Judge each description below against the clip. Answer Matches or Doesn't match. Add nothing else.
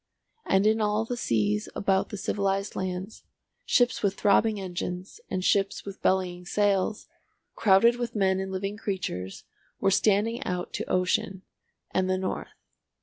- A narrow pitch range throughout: Matches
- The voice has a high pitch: Matches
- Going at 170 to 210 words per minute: Doesn't match